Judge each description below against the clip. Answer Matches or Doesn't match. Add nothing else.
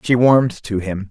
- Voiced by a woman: Doesn't match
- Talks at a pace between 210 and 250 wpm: Matches